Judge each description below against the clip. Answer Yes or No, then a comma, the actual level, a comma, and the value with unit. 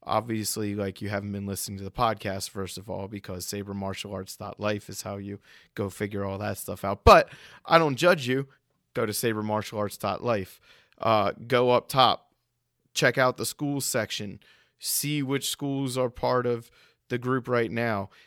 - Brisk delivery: No, average, 185 wpm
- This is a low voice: Yes, low, 110 Hz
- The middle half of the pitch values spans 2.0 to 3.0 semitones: No, average, 4.0 semitones